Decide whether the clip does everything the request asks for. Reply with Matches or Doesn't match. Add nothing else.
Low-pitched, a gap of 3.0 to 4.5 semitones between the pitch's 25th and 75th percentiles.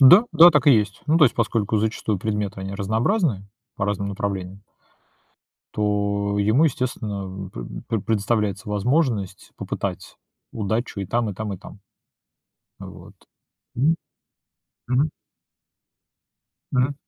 Matches